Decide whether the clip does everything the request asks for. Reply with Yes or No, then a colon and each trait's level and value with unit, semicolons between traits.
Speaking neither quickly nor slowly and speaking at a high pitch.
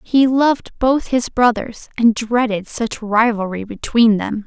Yes: average, 150 wpm; high, 230 Hz